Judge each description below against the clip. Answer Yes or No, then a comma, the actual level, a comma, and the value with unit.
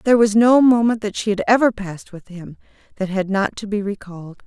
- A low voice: No, high, 205 Hz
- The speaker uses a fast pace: Yes, fast, 230 wpm